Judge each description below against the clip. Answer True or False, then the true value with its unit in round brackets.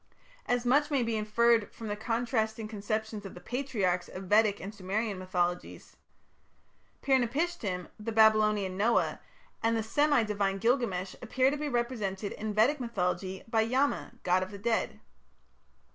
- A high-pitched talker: True (220 Hz)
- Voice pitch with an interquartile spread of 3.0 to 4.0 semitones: True (3.3 semitones)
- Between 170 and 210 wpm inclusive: False (150 wpm)